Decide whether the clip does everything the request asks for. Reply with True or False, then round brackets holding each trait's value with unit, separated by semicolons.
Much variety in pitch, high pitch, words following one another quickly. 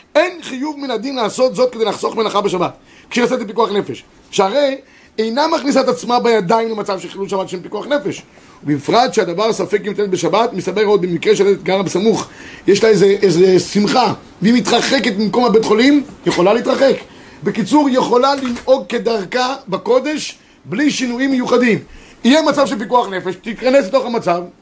False (4.5 semitones; 230 Hz; 165 wpm)